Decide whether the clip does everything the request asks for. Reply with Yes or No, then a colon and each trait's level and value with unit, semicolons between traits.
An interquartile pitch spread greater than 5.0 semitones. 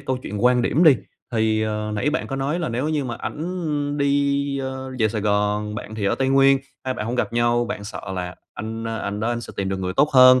No: average, 4.3 semitones